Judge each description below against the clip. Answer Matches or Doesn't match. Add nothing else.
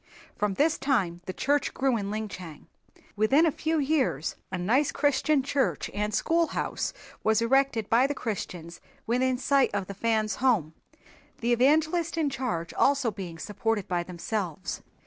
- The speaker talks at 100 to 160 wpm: Matches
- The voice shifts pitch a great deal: Matches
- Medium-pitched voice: Doesn't match